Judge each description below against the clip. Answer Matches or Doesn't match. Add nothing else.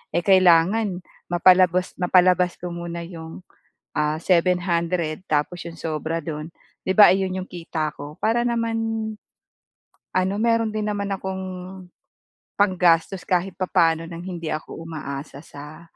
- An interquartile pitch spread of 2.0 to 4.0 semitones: Matches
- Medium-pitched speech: Matches